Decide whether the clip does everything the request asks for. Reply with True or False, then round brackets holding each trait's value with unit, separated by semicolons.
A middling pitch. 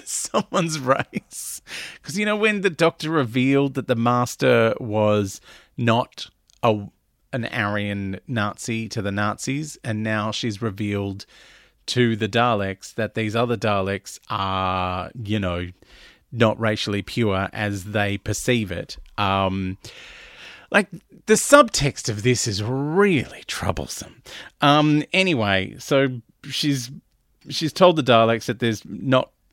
False (115 Hz)